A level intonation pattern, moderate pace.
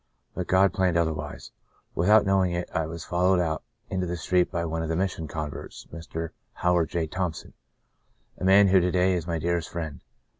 Yes: narrow, 2.2 semitones; average, 195 wpm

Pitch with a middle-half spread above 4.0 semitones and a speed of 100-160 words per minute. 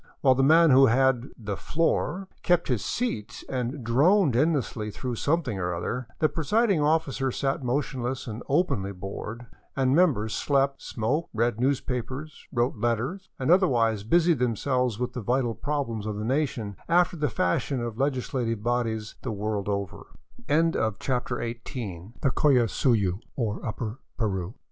Yes: average, 4.5 semitones; slow, 135 wpm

